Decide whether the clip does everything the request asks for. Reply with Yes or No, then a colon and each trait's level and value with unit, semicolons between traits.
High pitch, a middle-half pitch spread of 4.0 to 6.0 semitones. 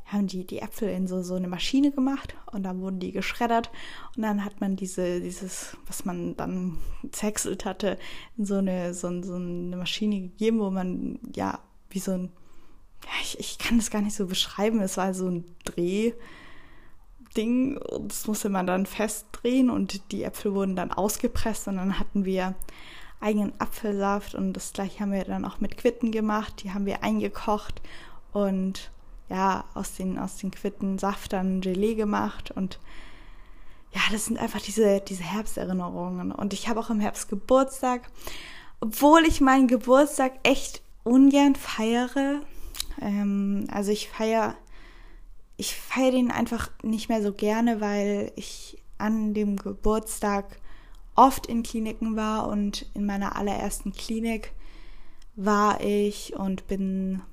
No: high, 205 Hz; average, 2.9 semitones